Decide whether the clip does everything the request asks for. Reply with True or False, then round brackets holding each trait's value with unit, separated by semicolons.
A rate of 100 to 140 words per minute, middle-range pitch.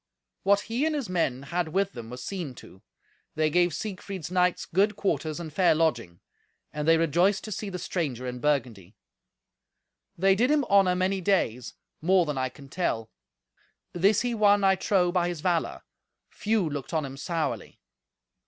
False (170 wpm; 175 Hz)